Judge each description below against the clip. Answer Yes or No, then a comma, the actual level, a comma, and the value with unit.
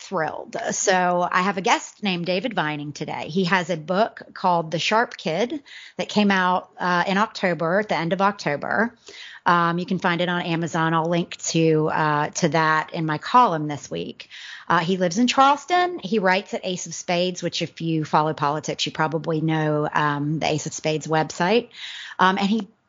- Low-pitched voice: No, medium, 175 Hz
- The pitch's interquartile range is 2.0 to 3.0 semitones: No, average, 4.0 semitones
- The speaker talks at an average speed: Yes, average, 195 wpm